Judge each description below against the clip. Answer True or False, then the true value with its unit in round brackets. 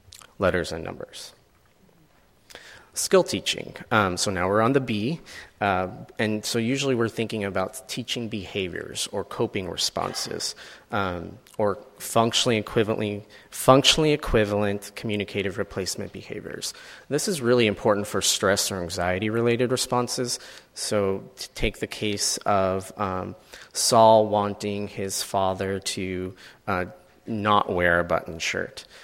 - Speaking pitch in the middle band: False (105 Hz)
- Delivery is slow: True (125 wpm)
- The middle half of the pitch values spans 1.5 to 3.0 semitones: False (3.5 semitones)